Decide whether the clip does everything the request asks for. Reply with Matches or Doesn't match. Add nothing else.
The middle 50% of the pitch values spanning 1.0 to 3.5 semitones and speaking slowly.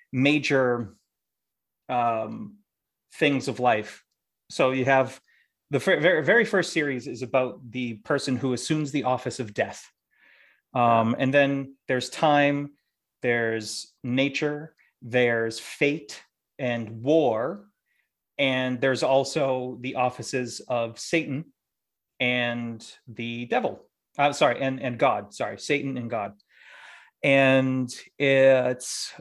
Matches